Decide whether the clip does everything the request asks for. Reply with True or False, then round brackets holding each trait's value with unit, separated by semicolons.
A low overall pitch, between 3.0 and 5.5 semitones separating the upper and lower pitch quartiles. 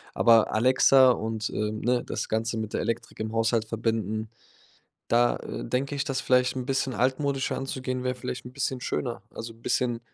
False (120 Hz; 2.4 semitones)